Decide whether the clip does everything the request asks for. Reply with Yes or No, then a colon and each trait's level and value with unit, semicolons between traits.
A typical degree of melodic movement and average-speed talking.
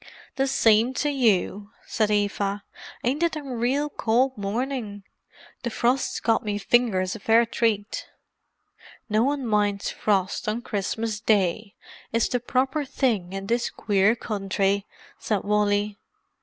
No: average, 3.3 semitones; slow, 130 wpm